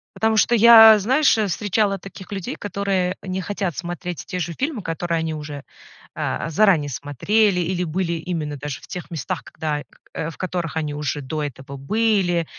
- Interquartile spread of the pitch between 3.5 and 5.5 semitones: Yes, average, 4.6 semitones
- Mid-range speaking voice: Yes, medium, 175 Hz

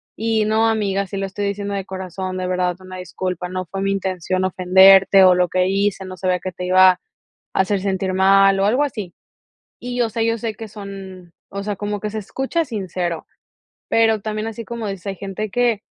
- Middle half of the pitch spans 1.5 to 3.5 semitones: Yes, narrow, 2.4 semitones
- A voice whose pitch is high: Yes, high, 195 Hz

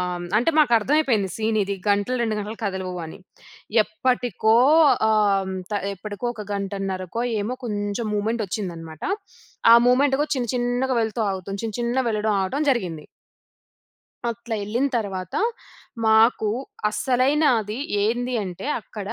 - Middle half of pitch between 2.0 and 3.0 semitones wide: No, average, 3.7 semitones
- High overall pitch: Yes, high, 215 Hz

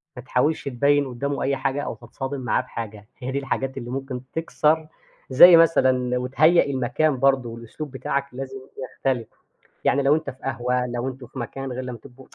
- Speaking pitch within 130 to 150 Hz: Yes, low, 135 Hz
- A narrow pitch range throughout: Yes, narrow, 2.0 semitones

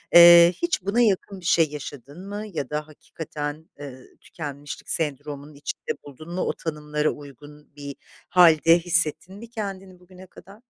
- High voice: No, medium, 160 Hz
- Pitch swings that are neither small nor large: Yes, average, 3.8 semitones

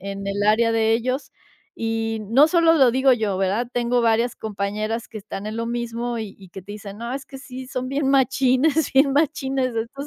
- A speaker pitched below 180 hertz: No, high, 235 Hz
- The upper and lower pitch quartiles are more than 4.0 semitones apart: No, average, 3.5 semitones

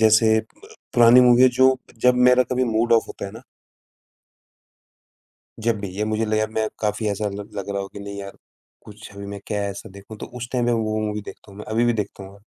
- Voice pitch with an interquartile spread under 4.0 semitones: Yes, narrow, 2.6 semitones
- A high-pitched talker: No, low, 110 Hz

